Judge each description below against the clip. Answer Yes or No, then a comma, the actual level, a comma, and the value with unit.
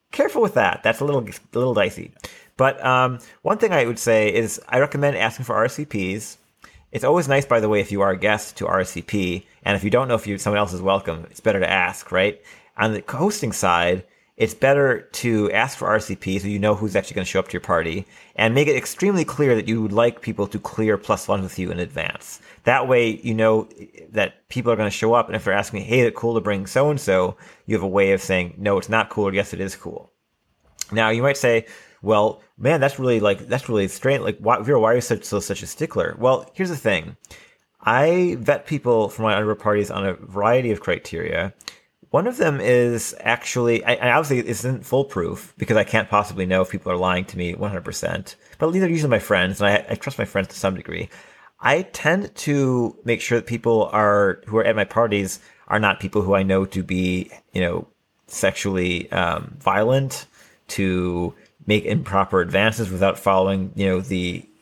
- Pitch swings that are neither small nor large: Yes, average, 3.8 semitones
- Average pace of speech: No, fast, 225 wpm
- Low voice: Yes, low, 105 Hz